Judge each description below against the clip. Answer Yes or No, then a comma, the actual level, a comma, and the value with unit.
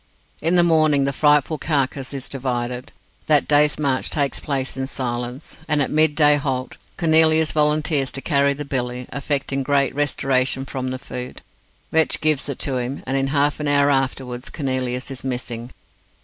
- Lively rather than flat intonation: No, narrow, 2.4 semitones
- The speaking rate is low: No, average, 165 wpm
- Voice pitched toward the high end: No, medium, 140 Hz